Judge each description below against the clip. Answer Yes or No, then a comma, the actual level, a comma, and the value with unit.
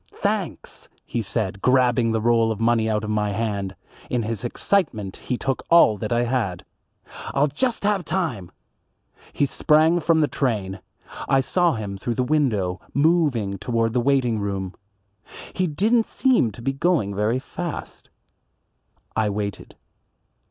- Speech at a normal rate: Yes, average, 145 wpm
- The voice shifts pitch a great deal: Yes, wide, 5.8 semitones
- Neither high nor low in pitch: No, low, 120 Hz